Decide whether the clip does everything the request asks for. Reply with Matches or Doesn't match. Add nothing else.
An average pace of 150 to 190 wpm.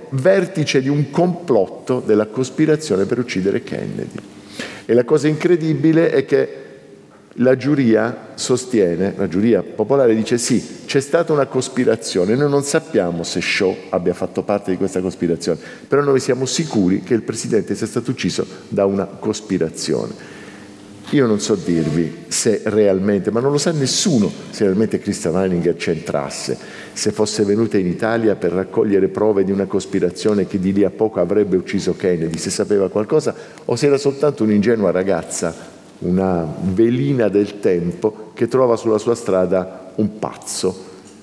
Matches